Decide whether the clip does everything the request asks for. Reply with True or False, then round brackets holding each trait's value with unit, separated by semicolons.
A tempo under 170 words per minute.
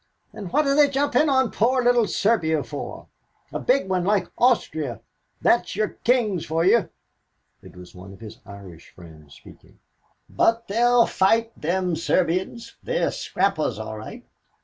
True (150 wpm)